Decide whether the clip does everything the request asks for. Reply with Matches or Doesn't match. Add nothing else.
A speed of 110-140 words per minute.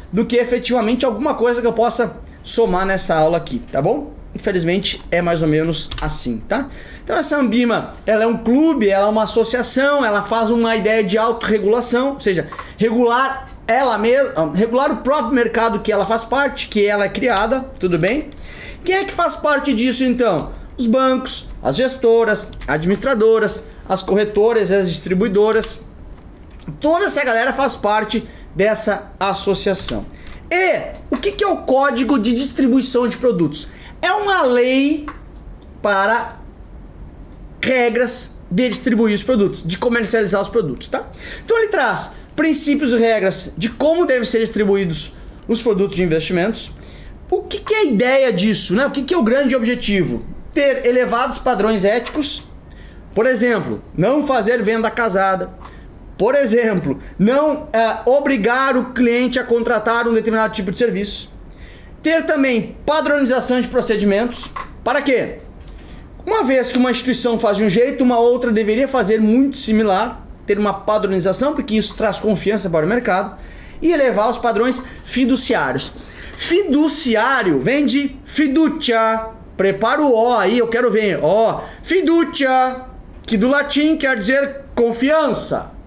Doesn't match